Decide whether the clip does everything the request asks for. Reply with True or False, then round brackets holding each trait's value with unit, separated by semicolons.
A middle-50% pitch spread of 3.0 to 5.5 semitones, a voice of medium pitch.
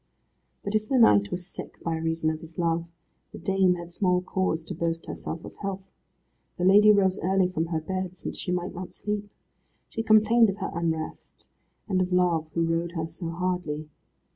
False (2.6 semitones; 180 Hz)